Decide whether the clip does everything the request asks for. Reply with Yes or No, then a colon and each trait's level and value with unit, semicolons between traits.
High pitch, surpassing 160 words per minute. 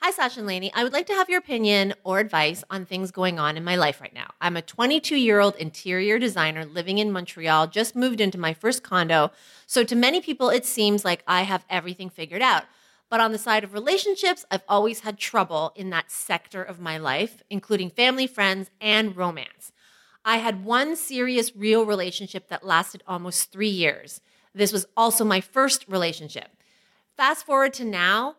Yes: high, 200 Hz; average, 195 wpm